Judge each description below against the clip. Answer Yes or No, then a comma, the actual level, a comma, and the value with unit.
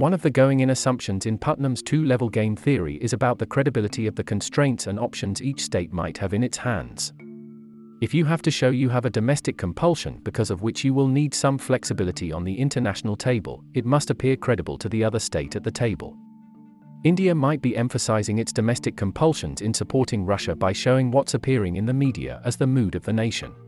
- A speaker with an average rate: No, fast, 215 wpm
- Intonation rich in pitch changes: No, average, 4.4 semitones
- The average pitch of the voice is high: No, low, 120 Hz